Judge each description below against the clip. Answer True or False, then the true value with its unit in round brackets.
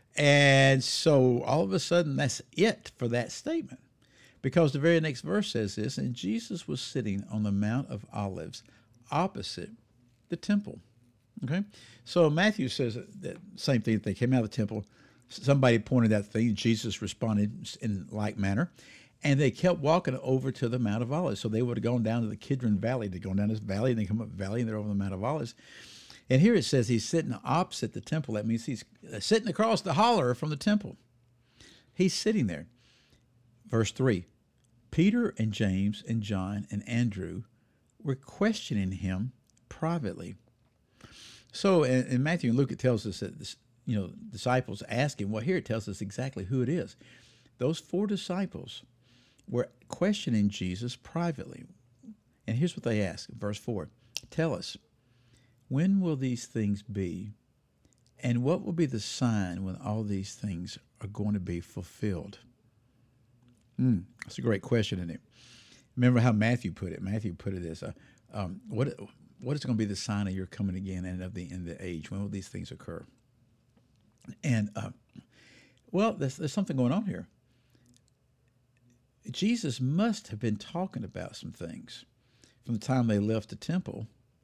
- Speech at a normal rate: True (180 wpm)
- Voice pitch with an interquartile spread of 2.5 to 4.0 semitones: False (4.4 semitones)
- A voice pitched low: True (120 Hz)